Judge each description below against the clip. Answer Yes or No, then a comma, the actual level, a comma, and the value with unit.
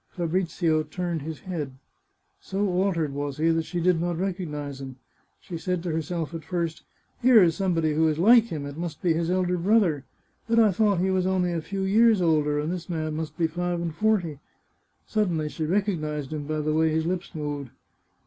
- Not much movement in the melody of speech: No, average, 3.0 semitones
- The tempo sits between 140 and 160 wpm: No, fast, 205 wpm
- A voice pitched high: No, medium, 170 Hz